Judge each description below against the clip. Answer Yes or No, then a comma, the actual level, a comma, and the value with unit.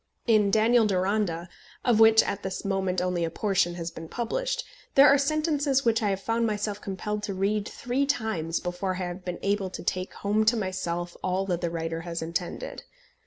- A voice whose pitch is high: Yes, high, 195 Hz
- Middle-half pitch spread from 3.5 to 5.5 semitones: Yes, average, 3.9 semitones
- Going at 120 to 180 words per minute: No, average, 195 wpm